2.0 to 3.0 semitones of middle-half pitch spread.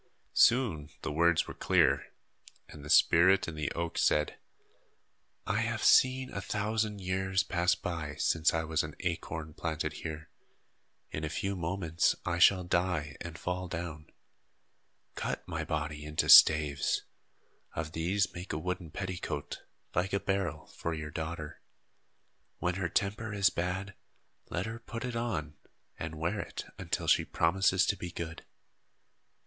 No: average, 3.6 semitones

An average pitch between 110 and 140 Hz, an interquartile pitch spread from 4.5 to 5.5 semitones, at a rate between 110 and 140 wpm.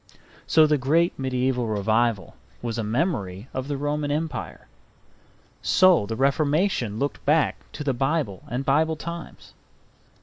Yes: low, 135 Hz; average, 4.8 semitones; slow, 135 wpm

